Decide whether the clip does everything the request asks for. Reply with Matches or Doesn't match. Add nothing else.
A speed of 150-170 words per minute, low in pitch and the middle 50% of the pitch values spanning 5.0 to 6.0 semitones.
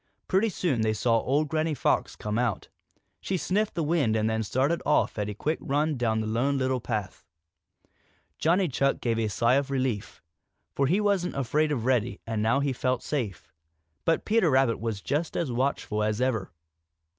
Doesn't match